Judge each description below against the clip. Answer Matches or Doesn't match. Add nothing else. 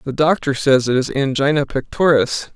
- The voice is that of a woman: Doesn't match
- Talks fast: Doesn't match